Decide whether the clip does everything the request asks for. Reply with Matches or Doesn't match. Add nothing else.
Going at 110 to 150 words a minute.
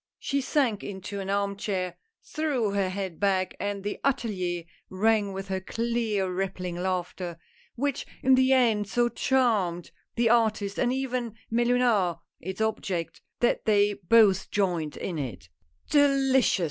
Doesn't match